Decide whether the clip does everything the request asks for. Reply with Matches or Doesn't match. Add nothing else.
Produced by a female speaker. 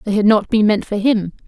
Matches